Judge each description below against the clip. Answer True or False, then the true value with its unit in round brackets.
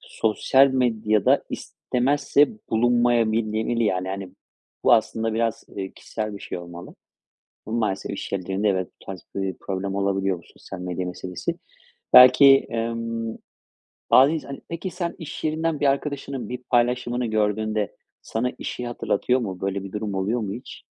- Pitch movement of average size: True (4.2 semitones)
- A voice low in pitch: True (110 Hz)